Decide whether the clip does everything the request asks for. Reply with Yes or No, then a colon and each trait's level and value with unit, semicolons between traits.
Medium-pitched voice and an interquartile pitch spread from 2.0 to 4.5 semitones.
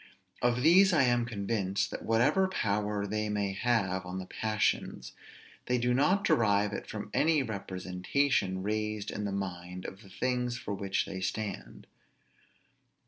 No: low, 105 Hz; average, 3.9 semitones